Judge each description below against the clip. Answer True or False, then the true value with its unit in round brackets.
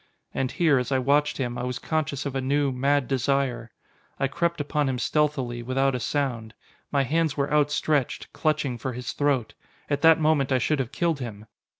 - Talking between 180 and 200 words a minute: True (195 wpm)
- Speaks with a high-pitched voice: False (135 Hz)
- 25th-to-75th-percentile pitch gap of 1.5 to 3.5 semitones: True (2.7 semitones)